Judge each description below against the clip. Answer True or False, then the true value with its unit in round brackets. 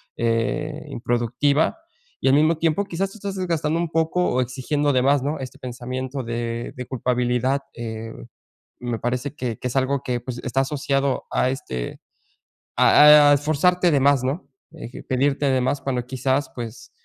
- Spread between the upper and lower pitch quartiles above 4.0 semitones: False (3.2 semitones)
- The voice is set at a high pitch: False (135 Hz)